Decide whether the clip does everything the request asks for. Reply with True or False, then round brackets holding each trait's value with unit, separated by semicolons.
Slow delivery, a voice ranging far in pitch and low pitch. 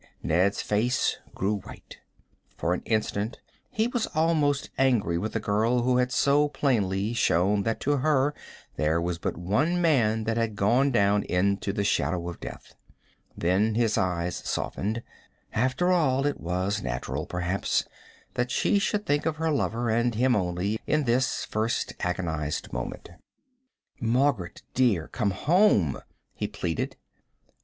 False (150 wpm; 6.2 semitones; 110 Hz)